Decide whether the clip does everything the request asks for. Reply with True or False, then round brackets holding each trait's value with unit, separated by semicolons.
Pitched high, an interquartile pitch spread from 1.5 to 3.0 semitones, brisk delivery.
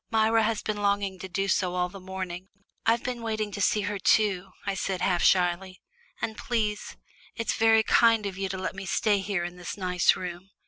True (195 Hz; 2.7 semitones; 210 wpm)